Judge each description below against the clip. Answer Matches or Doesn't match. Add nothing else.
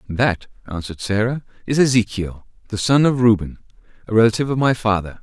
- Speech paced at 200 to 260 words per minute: Doesn't match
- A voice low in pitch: Matches